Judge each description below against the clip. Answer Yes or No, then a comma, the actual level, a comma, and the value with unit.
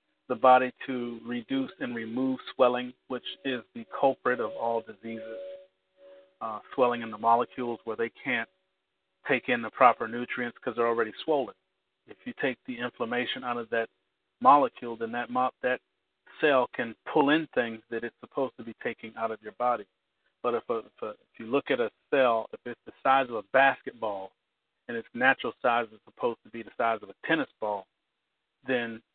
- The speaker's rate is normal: Yes, average, 190 wpm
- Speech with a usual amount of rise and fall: No, narrow, 1.9 semitones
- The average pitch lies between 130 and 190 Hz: No, low, 120 Hz